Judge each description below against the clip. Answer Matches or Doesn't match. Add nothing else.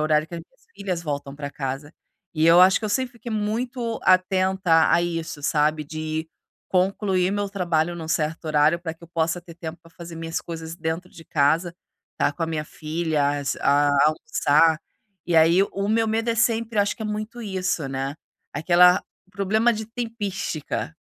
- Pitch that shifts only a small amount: Doesn't match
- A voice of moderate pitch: Matches